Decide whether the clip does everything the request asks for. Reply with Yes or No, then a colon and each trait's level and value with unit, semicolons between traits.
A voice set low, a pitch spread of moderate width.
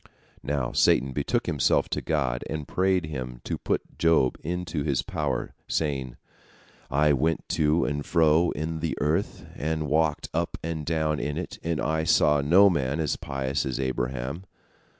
Yes: very low, 75 Hz; average, 3.0 semitones